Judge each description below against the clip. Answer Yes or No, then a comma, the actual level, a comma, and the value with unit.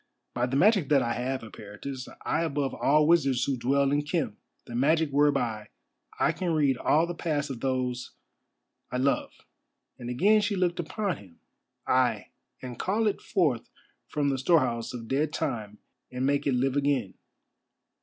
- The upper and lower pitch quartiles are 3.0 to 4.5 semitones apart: Yes, average, 4.1 semitones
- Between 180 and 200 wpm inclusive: No, average, 165 wpm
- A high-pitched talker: No, medium, 140 Hz